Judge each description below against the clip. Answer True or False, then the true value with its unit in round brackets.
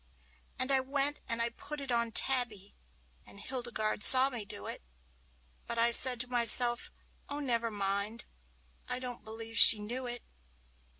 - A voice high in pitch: True (240 Hz)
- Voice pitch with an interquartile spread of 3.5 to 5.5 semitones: False (2.6 semitones)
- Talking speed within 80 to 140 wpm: False (155 wpm)